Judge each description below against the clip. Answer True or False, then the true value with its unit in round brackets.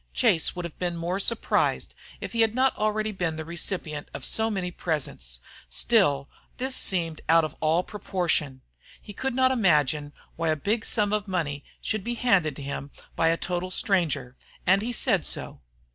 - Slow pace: False (175 wpm)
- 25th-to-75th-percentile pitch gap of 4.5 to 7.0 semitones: True (5.4 semitones)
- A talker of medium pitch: True (180 Hz)